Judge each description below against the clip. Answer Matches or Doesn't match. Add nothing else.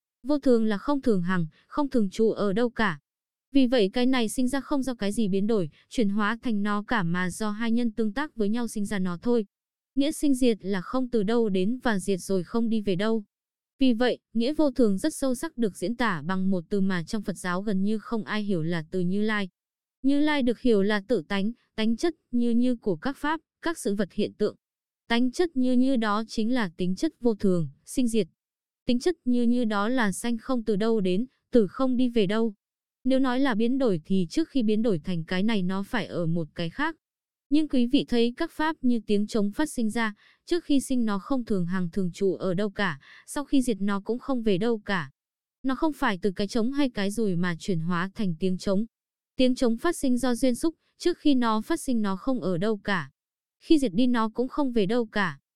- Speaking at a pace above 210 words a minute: Matches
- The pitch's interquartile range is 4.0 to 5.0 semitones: Matches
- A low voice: Doesn't match